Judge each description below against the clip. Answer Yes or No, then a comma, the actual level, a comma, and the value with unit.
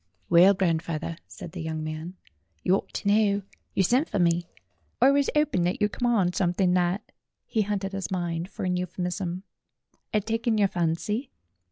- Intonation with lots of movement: No, average, 3.2 semitones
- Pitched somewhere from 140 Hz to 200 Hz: Yes, medium, 185 Hz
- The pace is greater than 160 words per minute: Yes, average, 175 wpm